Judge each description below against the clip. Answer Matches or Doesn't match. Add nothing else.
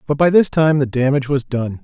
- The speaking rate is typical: Doesn't match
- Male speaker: Matches